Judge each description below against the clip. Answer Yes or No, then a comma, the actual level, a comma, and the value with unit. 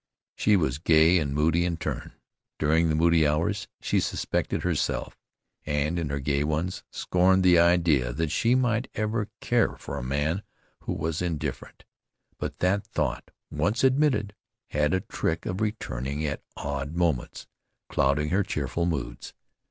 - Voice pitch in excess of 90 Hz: No, very low, 80 Hz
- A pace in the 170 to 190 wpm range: No, average, 150 wpm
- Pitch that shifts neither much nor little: Yes, average, 4.0 semitones